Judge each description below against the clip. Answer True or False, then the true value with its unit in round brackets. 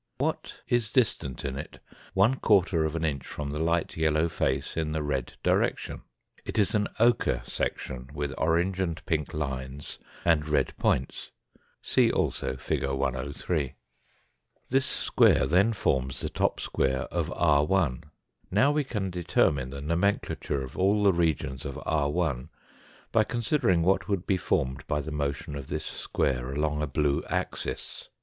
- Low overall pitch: True (75 Hz)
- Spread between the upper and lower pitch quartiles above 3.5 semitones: True (5.3 semitones)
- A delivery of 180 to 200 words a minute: False (155 wpm)